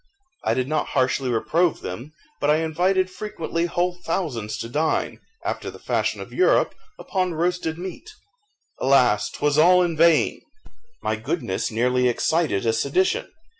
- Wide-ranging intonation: Yes, wide, 5.7 semitones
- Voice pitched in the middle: Yes, medium, 160 Hz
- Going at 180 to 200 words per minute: No, average, 145 wpm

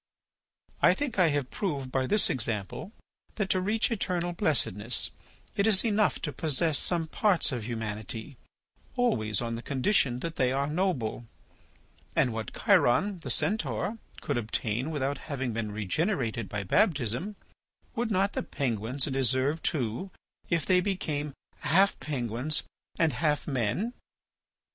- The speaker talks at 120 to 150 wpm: Yes, average, 140 wpm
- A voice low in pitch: No, medium, 145 Hz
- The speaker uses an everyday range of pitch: No, wide, 7.4 semitones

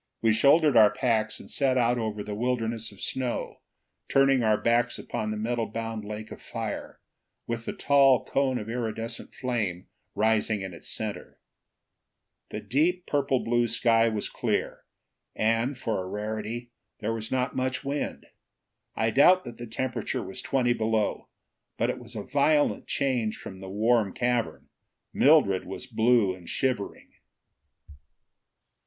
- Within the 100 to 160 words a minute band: Yes, average, 150 wpm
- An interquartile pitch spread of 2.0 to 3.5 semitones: Yes, average, 2.9 semitones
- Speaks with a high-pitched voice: No, low, 115 Hz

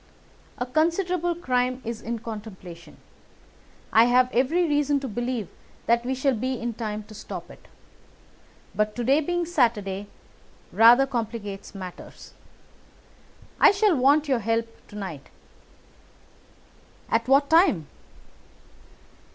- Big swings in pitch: No, average, 4.6 semitones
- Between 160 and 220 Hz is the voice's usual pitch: No, high, 245 Hz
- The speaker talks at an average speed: No, slow, 120 wpm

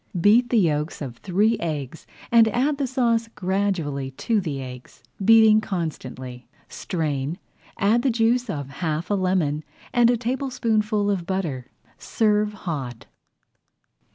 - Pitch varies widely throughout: Yes, wide, 7.1 semitones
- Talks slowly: Yes, slow, 130 wpm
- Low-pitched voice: No, high, 195 Hz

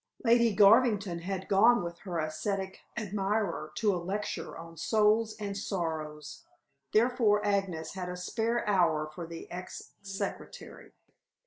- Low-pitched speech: No, high, 195 Hz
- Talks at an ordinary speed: No, slow, 130 wpm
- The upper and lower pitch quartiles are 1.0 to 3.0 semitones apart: No, average, 3.7 semitones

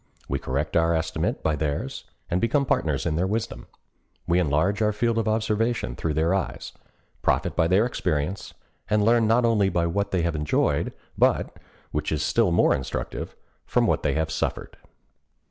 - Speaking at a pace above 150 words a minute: Yes, average, 165 wpm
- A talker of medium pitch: No, very low, 90 Hz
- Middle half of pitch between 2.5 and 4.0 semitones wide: No, wide, 5.5 semitones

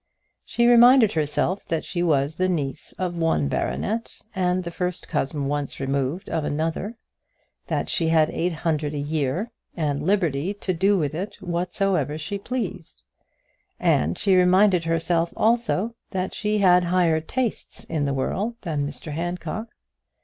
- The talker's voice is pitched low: No, medium, 170 Hz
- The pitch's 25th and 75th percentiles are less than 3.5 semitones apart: No, average, 4.2 semitones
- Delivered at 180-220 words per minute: No, average, 150 wpm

